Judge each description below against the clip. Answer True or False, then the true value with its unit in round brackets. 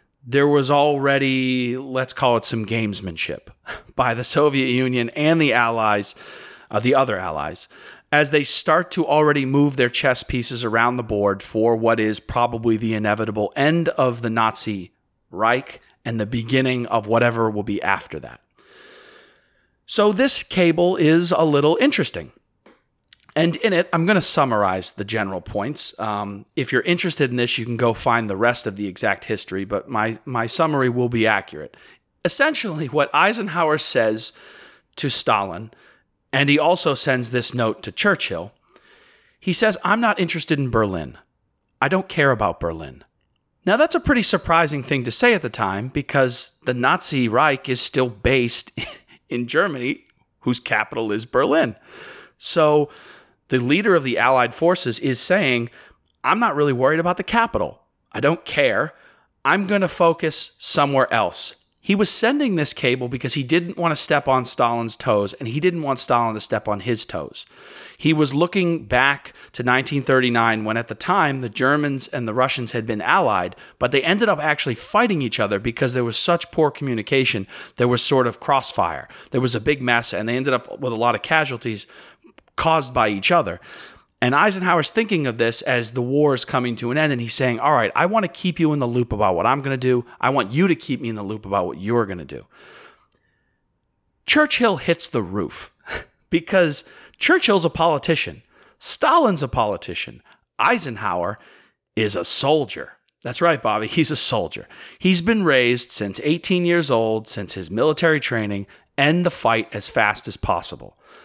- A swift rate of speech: False (180 wpm)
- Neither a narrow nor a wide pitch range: False (6.0 semitones)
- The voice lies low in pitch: True (130 Hz)